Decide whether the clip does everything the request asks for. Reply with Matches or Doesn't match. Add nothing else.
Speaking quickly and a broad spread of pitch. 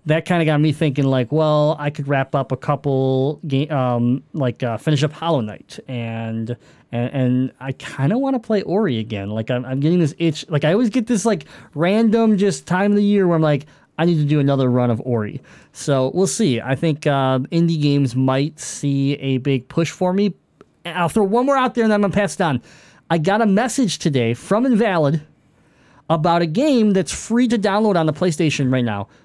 Matches